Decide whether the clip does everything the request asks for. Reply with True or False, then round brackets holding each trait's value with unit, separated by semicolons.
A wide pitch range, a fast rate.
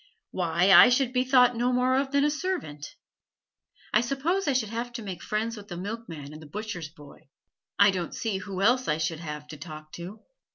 True (7.1 semitones; 210 wpm)